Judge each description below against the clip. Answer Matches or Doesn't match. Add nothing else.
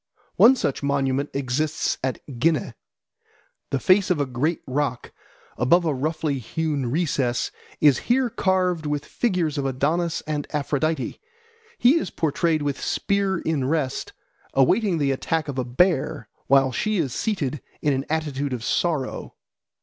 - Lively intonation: Doesn't match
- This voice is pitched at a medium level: Matches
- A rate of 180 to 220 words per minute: Doesn't match